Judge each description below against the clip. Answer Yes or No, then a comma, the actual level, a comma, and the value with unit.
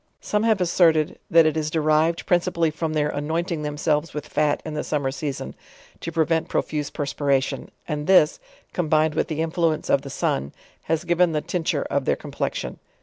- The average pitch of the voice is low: No, medium, 155 Hz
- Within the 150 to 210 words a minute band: Yes, average, 185 wpm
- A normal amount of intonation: No, narrow, 1.9 semitones